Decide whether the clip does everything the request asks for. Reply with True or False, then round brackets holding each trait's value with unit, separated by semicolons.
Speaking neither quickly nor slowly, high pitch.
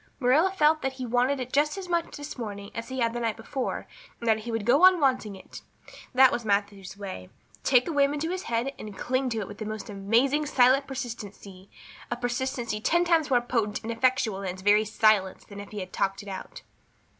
False (225 wpm; 240 Hz)